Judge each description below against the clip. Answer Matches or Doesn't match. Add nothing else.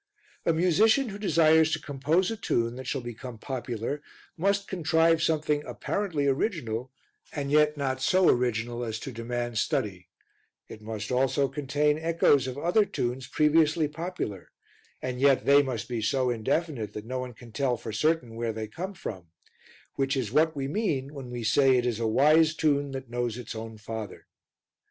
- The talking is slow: Doesn't match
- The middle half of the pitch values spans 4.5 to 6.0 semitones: Matches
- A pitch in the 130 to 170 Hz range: Matches